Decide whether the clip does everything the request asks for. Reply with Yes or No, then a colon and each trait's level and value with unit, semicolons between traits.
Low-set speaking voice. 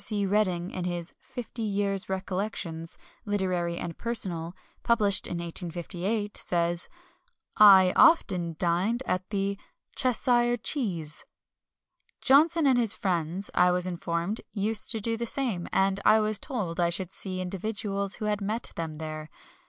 No: high, 195 Hz